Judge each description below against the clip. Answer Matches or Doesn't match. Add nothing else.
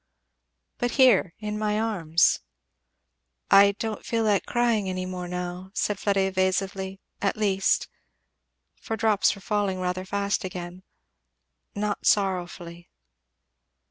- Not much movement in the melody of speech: Matches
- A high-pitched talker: Matches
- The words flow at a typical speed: Doesn't match